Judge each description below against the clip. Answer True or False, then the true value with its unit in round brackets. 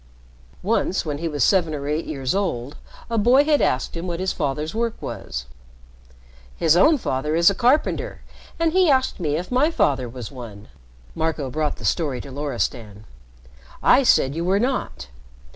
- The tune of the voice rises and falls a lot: True (8.0 semitones)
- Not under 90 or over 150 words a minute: False (175 wpm)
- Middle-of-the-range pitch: True (160 Hz)